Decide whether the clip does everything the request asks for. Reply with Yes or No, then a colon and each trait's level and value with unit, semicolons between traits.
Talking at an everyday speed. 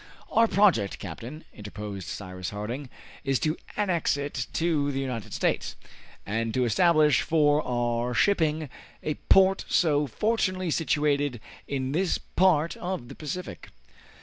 No: slow, 130 wpm